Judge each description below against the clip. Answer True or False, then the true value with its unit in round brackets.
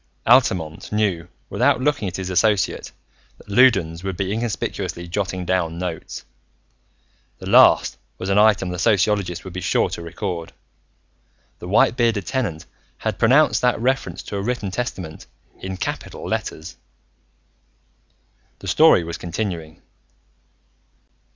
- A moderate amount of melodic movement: True (4.0 semitones)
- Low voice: True (95 Hz)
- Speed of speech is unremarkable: False (130 wpm)